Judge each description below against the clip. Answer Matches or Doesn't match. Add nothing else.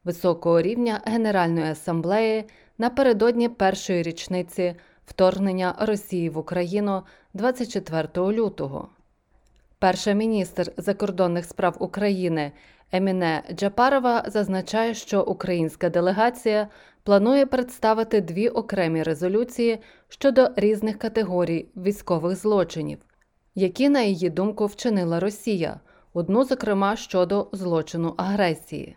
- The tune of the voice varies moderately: Matches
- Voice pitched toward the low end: Doesn't match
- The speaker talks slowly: Matches